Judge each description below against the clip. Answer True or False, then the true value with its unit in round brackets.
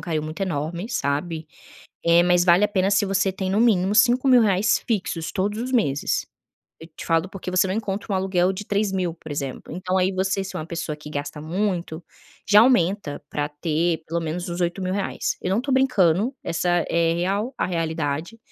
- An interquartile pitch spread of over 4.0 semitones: False (3.5 semitones)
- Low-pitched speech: False (185 Hz)